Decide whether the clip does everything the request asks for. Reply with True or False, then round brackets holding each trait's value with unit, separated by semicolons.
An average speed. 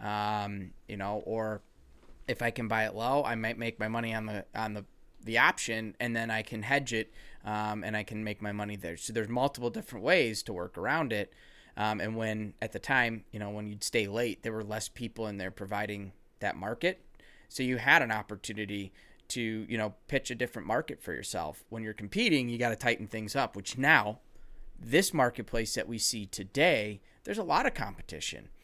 False (210 wpm)